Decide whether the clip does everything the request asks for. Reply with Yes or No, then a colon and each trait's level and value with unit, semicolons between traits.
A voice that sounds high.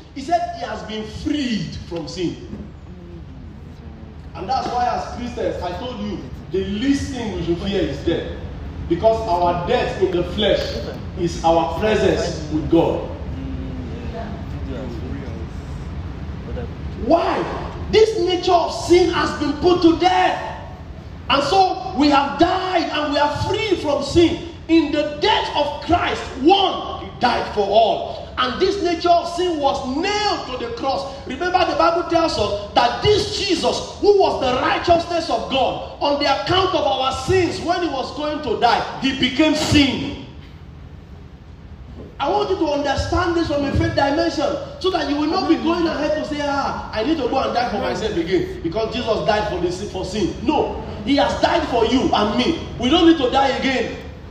Yes: very high, 285 Hz